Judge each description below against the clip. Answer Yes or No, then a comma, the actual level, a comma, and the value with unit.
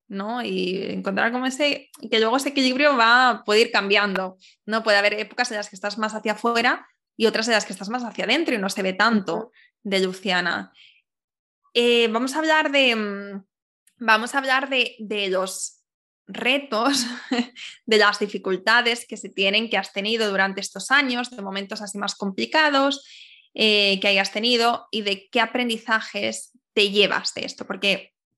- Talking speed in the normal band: Yes, average, 175 wpm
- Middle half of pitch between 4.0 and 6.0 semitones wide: No, average, 3.6 semitones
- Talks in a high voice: Yes, high, 220 Hz